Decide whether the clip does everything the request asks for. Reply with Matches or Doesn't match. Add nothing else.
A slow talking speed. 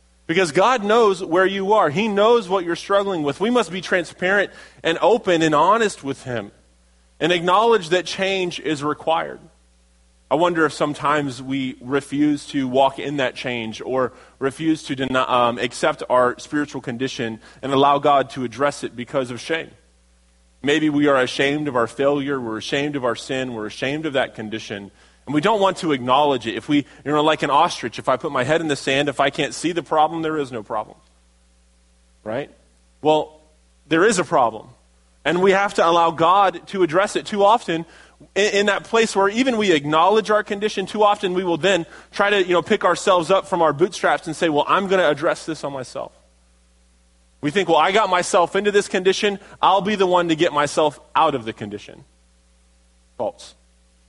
Doesn't match